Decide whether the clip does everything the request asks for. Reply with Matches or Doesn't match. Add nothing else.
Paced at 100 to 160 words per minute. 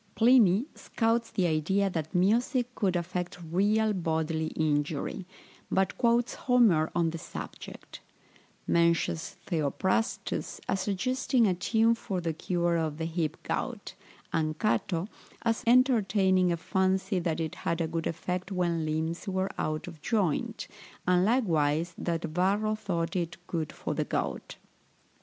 Matches